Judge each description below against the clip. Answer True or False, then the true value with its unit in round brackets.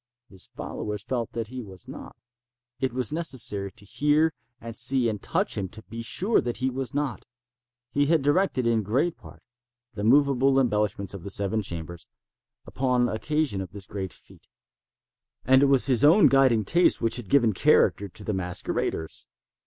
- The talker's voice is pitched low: True (120 Hz)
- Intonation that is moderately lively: True (5.0 semitones)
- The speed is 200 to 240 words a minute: False (175 wpm)